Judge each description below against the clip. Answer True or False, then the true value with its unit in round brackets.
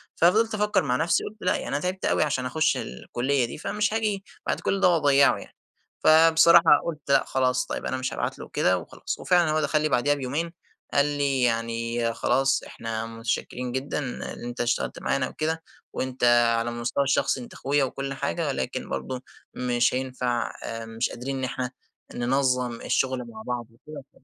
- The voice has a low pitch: True (130 Hz)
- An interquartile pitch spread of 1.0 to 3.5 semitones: False (4.0 semitones)